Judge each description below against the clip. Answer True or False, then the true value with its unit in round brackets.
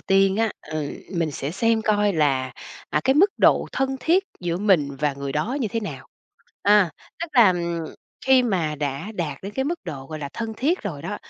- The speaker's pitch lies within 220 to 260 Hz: False (190 Hz)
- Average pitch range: False (7.3 semitones)